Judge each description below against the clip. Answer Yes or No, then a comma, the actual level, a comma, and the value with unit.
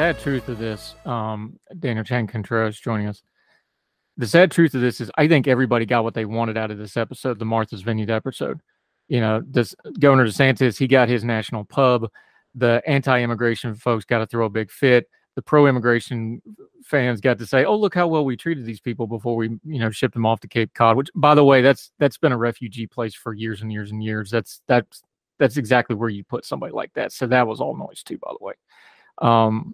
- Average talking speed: No, fast, 220 wpm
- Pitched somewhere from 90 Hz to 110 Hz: No, low, 120 Hz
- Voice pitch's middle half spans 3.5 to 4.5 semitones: No, average, 3.0 semitones